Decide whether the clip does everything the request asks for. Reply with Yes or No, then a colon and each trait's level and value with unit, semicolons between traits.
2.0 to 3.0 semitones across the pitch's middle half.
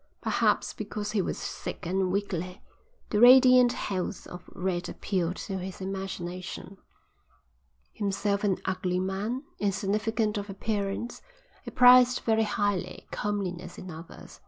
Yes: narrow, 2.5 semitones